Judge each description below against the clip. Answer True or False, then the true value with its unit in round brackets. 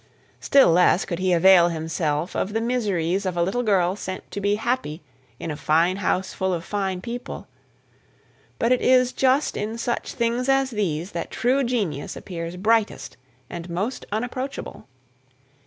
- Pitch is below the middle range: False (195 Hz)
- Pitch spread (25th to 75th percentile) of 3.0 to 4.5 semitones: False (5.5 semitones)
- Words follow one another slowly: False (160 wpm)